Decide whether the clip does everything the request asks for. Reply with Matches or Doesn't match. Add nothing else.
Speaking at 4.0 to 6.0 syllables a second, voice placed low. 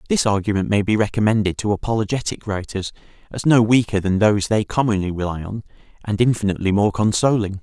Doesn't match